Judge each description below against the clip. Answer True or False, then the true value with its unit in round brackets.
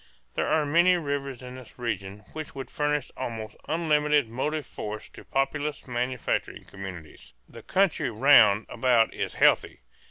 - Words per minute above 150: False (140 wpm)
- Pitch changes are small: False (4.7 semitones)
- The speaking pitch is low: True (130 Hz)